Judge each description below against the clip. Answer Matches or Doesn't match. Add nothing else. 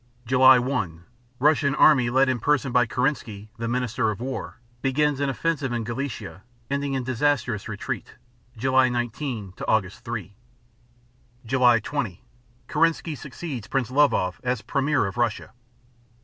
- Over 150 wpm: Doesn't match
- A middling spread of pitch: Matches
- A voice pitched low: Matches